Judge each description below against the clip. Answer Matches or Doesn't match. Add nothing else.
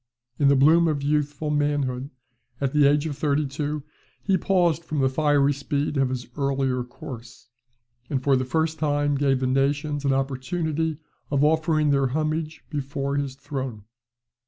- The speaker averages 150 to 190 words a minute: Matches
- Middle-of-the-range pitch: Matches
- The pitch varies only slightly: Matches